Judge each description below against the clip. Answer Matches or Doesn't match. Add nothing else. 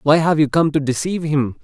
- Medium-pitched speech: Matches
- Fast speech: Matches